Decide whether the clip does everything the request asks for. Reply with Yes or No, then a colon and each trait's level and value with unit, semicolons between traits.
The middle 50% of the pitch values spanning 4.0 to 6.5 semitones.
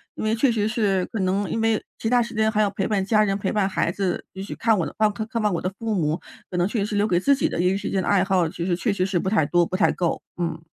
No: average, 3.0 semitones